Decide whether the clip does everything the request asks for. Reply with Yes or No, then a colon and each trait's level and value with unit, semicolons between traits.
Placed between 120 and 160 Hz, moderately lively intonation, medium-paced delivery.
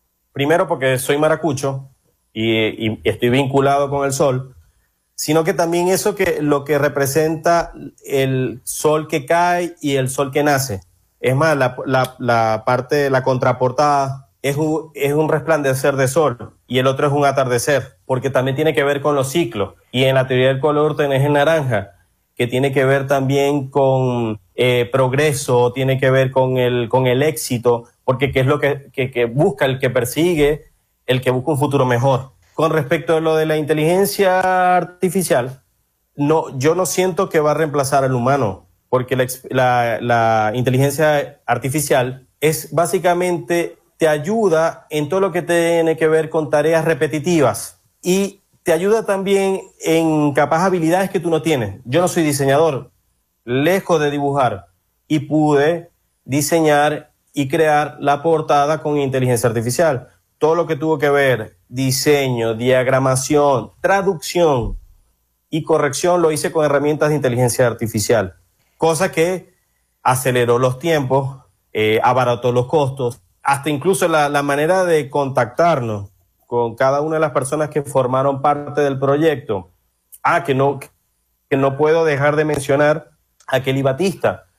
Yes: medium, 140 Hz; average, 3.8 semitones; average, 155 wpm